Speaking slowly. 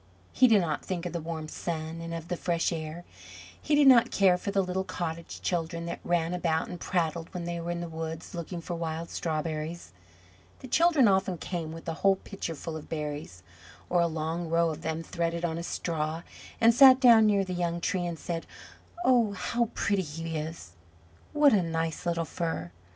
No: average, 200 wpm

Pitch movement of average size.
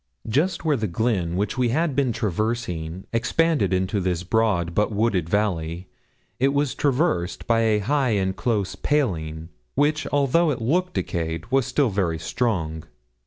No: wide, 7.2 semitones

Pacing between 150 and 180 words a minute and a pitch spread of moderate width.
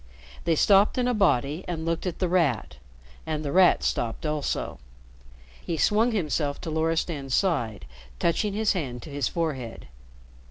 Yes: average, 155 wpm; average, 4.7 semitones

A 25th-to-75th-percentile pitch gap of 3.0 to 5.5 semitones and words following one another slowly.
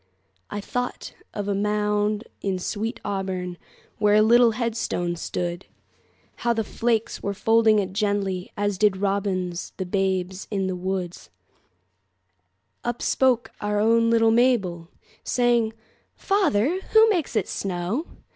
Yes: average, 3.7 semitones; slow, 115 wpm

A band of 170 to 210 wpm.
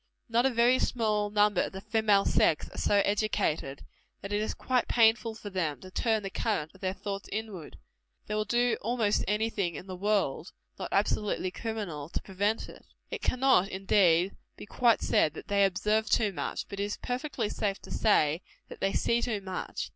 Yes: average, 195 wpm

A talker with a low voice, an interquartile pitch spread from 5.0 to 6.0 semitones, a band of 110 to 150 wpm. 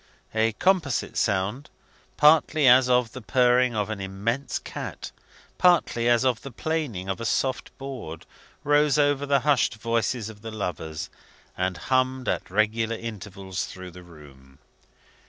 Yes: low, 115 Hz; average, 5.3 semitones; average, 145 wpm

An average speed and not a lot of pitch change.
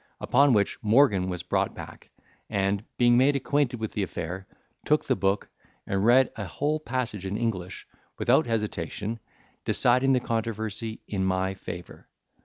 No: average, 150 wpm; average, 4.1 semitones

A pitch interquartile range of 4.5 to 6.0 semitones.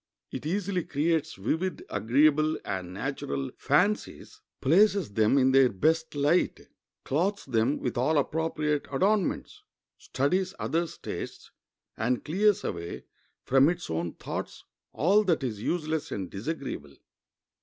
Yes: wide, 5.5 semitones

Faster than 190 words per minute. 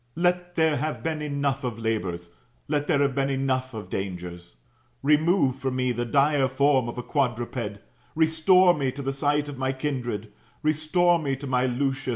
No: average, 185 wpm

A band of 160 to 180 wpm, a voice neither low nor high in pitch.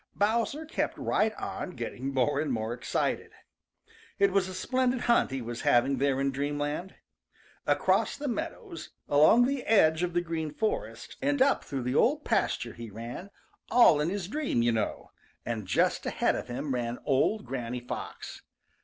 Yes: average, 170 wpm; medium, 150 Hz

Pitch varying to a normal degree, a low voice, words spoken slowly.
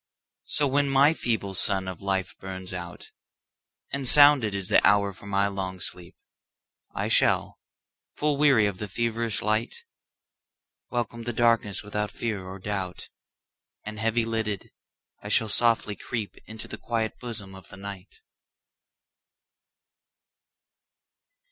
Yes: average, 3.3 semitones; low, 105 Hz; slow, 115 wpm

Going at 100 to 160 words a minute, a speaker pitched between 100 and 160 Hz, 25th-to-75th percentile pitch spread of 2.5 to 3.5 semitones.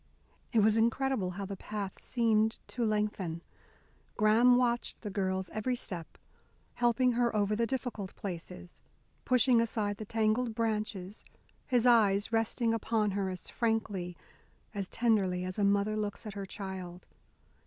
No: average, 145 wpm; high, 215 Hz; average, 2.9 semitones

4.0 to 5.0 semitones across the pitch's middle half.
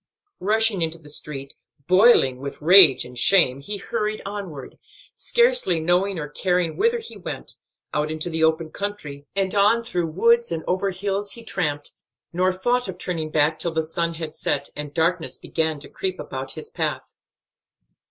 Yes: average, 4.5 semitones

